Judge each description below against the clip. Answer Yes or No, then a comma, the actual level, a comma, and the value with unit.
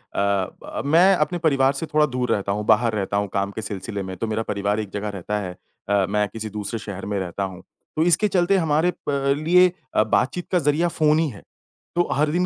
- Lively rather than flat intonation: Yes, wide, 7.7 semitones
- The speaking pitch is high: No, low, 110 Hz